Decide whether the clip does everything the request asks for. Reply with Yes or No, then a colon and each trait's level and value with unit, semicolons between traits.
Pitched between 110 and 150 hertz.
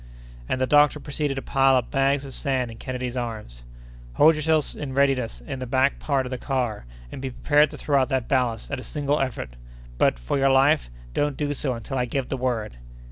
Yes: low, 135 Hz